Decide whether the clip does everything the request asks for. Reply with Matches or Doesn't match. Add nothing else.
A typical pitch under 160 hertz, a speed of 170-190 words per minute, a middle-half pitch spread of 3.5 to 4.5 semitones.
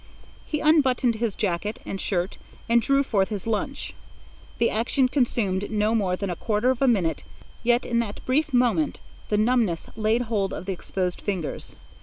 Doesn't match